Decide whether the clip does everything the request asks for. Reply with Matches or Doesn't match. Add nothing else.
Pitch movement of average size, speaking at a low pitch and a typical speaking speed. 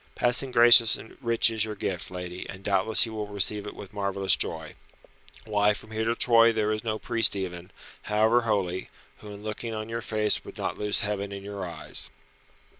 Doesn't match